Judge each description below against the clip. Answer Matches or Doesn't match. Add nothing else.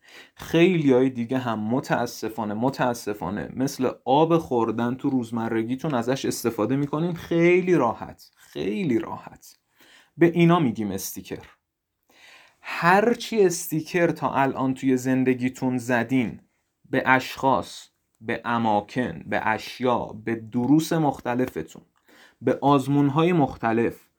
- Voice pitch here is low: Matches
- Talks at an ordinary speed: Doesn't match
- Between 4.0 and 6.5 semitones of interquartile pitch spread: Matches